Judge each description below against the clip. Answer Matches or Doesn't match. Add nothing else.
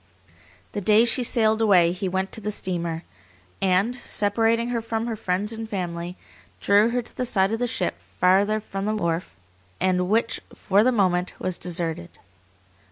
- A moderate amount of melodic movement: Matches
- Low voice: Doesn't match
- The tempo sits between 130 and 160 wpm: Doesn't match